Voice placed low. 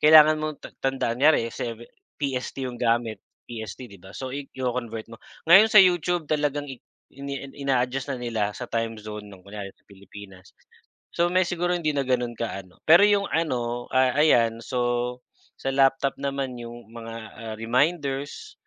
Yes: low, 125 Hz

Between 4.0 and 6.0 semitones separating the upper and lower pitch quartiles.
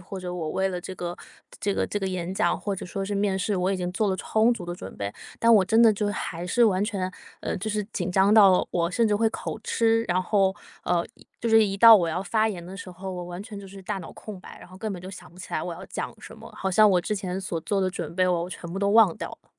No: narrow, 2.6 semitones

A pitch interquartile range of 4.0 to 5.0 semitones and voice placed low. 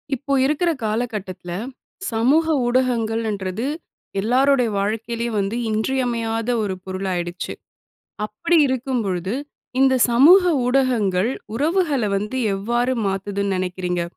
No: average, 4.7 semitones; high, 225 Hz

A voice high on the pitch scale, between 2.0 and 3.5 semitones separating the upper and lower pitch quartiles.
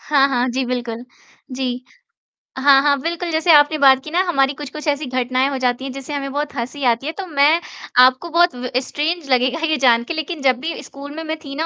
Yes: very high, 275 Hz; average, 3.2 semitones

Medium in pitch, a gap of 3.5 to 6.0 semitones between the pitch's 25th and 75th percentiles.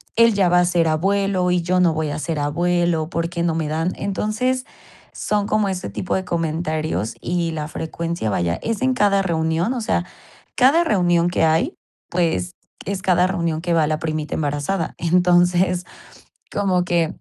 No: medium, 175 Hz; average, 2.8 semitones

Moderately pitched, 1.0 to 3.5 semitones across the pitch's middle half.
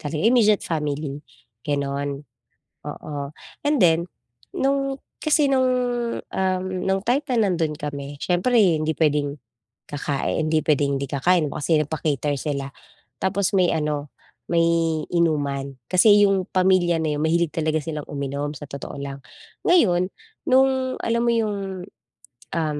No: medium, 160 Hz; average, 5.0 semitones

